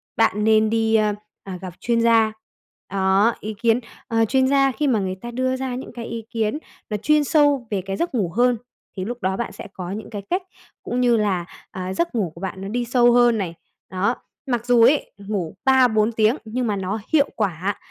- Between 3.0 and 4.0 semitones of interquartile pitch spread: Yes, average, 3.5 semitones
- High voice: Yes, high, 225 Hz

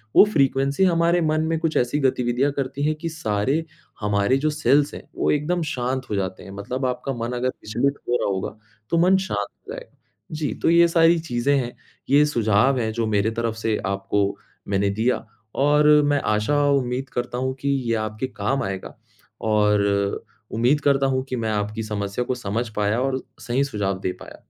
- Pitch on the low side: Yes, low, 125 Hz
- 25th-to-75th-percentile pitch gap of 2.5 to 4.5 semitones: No, average, 5.2 semitones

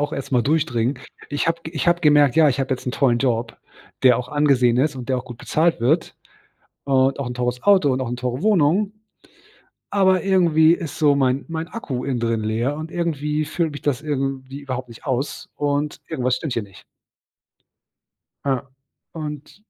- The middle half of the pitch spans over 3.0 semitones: Yes, average, 3.8 semitones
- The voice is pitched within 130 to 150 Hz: Yes, medium, 140 Hz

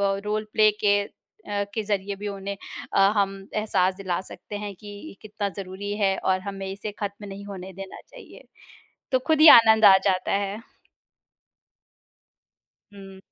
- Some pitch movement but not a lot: No, narrow, 1.3 semitones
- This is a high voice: Yes, high, 200 Hz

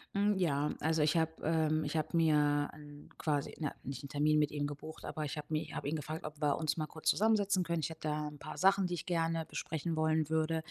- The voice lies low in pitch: No, medium, 155 Hz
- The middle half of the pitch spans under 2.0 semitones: Yes, narrow, 1.6 semitones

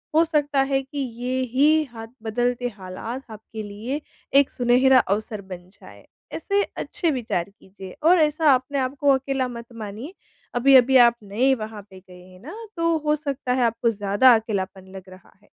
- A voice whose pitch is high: Yes, high, 245 Hz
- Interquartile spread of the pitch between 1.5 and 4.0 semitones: No, average, 4.6 semitones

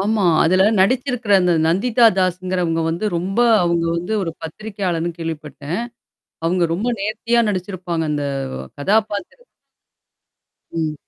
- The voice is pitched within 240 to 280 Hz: No, medium, 185 Hz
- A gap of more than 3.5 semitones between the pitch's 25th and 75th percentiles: Yes, average, 4.0 semitones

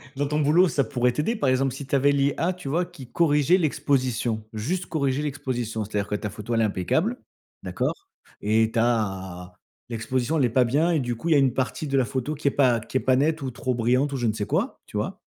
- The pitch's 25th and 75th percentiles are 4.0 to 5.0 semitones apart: Yes, average, 4.3 semitones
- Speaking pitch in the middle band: No, low, 130 Hz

